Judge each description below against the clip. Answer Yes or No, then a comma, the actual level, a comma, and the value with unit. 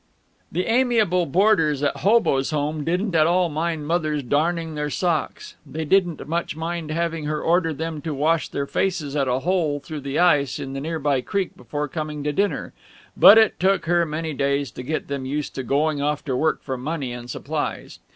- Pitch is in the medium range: Yes, medium, 155 Hz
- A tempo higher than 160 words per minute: Yes, average, 200 wpm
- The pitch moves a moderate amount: Yes, average, 3.1 semitones